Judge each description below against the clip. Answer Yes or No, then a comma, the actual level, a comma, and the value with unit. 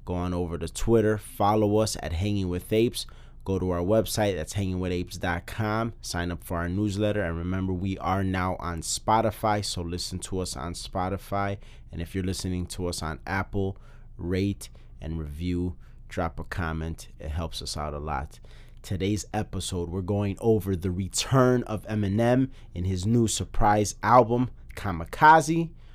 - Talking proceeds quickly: No, average, 160 wpm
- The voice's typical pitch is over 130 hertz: No, very low, 95 Hz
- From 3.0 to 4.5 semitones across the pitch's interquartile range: Yes, average, 3.4 semitones